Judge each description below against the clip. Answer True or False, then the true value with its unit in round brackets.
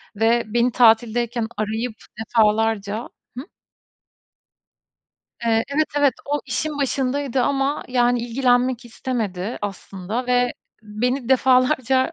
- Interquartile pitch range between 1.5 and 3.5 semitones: True (2.7 semitones)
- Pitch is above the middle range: True (245 Hz)